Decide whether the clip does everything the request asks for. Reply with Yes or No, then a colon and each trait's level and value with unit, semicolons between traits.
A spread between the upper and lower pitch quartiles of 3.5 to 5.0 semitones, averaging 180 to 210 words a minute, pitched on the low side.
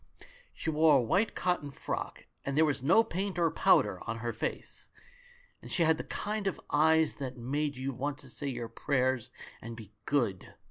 No: average, 4.1 semitones; average, 190 wpm; medium, 145 Hz